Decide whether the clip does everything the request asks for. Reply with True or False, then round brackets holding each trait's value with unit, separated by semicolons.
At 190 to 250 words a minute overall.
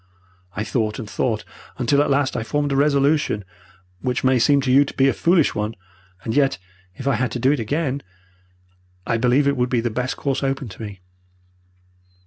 True (200 wpm)